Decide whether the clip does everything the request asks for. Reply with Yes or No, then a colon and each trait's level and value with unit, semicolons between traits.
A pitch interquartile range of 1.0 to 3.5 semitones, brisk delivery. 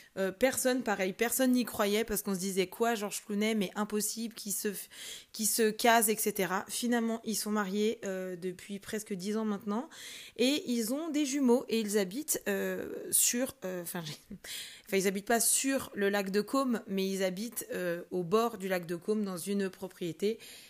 No: average, 3.2 semitones; average, 180 wpm